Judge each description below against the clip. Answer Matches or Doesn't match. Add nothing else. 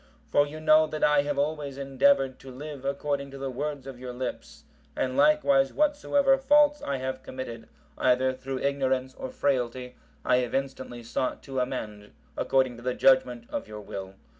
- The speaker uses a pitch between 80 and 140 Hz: Matches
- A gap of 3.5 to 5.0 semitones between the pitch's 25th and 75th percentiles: Doesn't match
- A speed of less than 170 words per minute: Doesn't match